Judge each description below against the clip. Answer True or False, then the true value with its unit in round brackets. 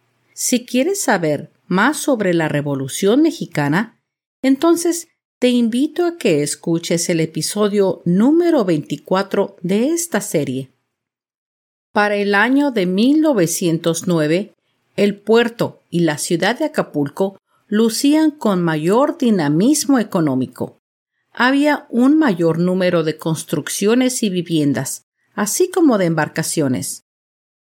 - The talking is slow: True (110 wpm)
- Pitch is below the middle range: False (195 Hz)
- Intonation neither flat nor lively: False (7.7 semitones)